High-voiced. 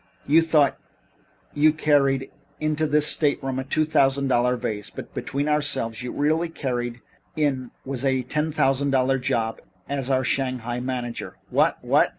No: low, 135 Hz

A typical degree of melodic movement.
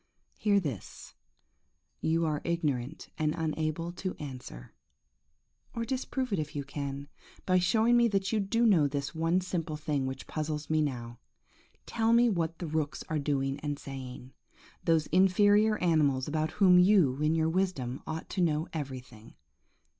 Yes: average, 4.6 semitones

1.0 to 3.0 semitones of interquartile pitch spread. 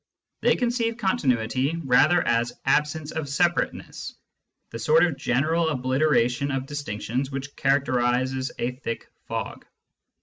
No: average, 4.0 semitones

